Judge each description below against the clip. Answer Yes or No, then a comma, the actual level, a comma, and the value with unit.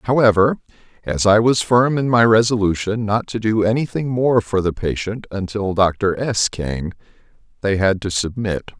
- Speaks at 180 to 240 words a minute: No, average, 170 wpm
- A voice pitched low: Yes, low, 105 Hz